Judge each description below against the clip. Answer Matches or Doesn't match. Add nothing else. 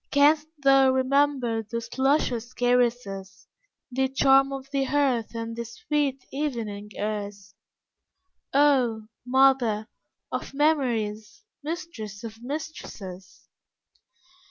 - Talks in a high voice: Matches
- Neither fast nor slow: Doesn't match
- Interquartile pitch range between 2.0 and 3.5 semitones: Doesn't match